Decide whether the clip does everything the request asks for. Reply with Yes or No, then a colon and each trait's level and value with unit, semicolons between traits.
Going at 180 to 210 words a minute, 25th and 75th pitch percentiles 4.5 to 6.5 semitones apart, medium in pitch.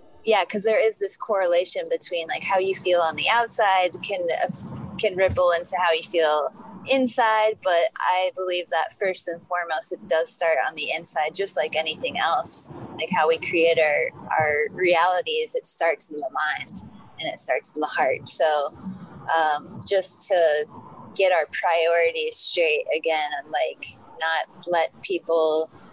No: average, 165 wpm; average, 5.2 semitones; medium, 180 Hz